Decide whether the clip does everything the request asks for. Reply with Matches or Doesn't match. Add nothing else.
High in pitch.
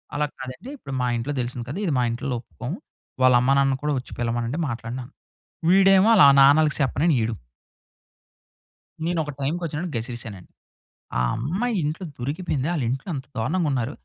Doesn't match